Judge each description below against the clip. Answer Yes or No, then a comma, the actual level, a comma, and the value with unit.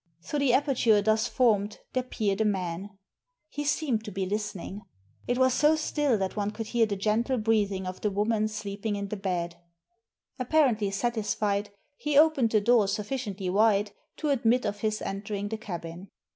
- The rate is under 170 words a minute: No, average, 175 wpm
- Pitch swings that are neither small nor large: Yes, average, 3.1 semitones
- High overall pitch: Yes, high, 215 Hz